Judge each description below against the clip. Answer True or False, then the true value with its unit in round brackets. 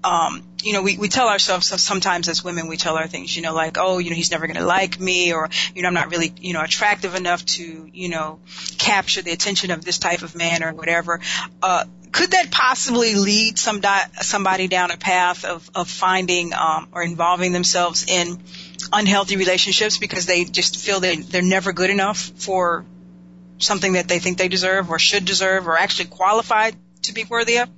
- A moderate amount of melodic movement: False (2.1 semitones)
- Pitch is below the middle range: False (180 Hz)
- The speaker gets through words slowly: False (205 wpm)